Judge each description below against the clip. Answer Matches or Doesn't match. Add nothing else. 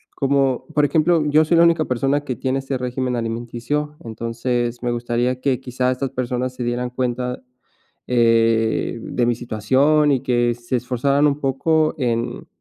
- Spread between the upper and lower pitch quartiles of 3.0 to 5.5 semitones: Doesn't match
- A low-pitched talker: Matches